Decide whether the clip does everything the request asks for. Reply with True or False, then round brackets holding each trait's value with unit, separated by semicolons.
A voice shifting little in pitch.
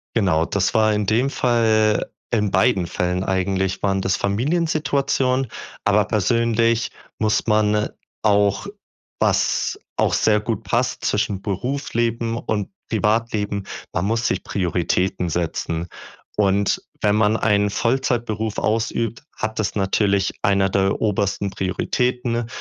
False (3.1 semitones)